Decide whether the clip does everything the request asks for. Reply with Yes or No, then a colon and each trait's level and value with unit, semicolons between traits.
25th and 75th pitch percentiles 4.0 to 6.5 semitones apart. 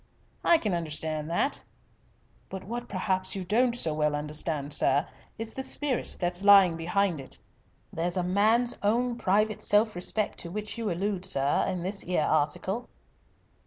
Yes: average, 4.4 semitones